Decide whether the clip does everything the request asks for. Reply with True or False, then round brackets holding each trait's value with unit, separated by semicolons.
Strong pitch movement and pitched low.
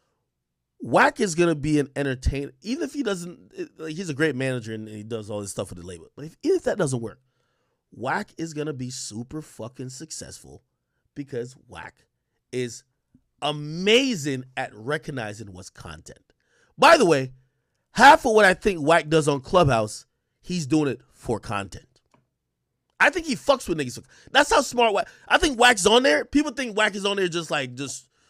False (7.8 semitones; 150 Hz)